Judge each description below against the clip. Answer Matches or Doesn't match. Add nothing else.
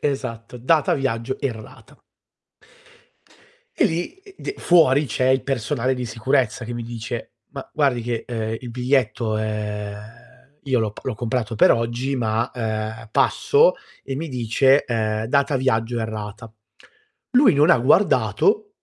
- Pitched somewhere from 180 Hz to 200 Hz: Doesn't match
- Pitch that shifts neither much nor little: Matches